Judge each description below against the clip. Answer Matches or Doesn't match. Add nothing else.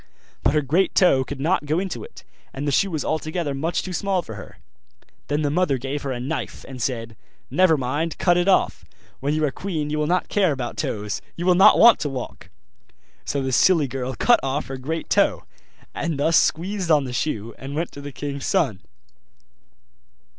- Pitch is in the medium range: Matches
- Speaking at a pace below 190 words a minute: Doesn't match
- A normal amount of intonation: Matches